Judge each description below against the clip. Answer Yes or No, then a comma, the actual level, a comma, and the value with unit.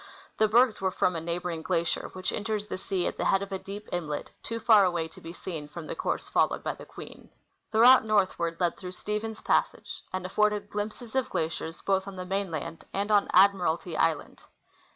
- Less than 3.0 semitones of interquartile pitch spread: No, average, 3.7 semitones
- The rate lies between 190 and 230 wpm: Yes, fast, 205 wpm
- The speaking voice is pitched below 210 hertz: Yes, high, 190 Hz